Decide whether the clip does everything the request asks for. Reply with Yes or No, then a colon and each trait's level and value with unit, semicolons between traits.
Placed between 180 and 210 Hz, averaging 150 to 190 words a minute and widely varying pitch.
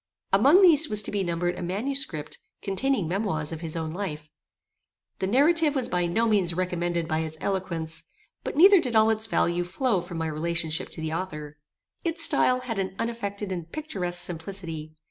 Yes: medium, 185 Hz; average, 180 wpm; wide, 5.8 semitones